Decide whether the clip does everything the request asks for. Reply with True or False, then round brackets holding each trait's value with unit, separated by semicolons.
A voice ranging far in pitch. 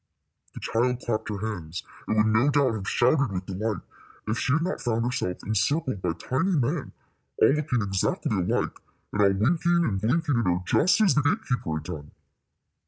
True (6.4 semitones)